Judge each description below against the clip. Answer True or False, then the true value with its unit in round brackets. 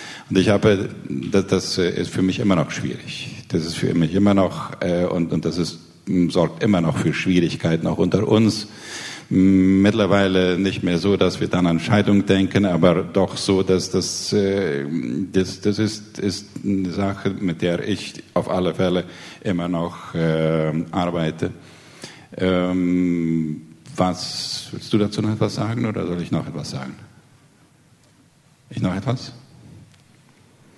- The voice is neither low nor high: False (95 Hz)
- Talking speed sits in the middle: True (155 wpm)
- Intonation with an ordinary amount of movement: False (2.3 semitones)